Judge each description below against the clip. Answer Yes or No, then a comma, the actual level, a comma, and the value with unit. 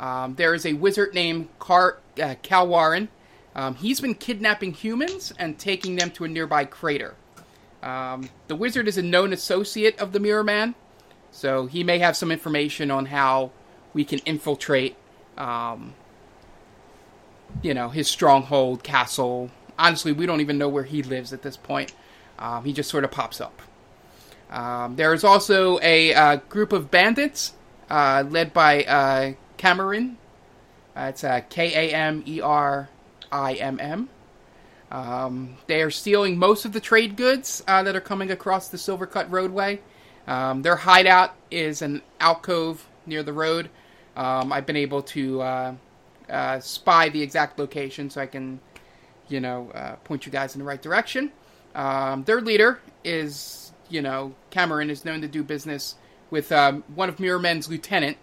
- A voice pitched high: No, medium, 155 Hz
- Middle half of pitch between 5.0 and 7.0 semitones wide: Yes, average, 5.3 semitones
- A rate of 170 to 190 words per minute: No, average, 160 wpm